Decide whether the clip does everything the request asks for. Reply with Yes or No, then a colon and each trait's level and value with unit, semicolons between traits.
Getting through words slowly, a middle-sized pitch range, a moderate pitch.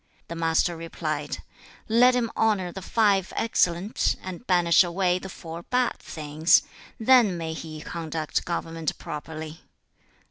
Yes: slow, 130 wpm; average, 3.5 semitones; medium, 170 Hz